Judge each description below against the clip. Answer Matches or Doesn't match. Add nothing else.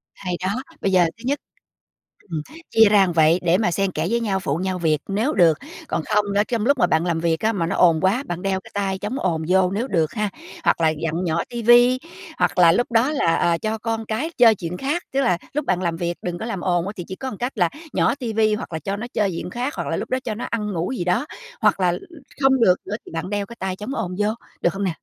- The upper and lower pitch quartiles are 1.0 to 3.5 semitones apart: Doesn't match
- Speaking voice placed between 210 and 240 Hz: Doesn't match